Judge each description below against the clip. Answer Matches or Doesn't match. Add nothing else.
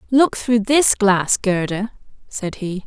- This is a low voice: Doesn't match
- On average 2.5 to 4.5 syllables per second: Matches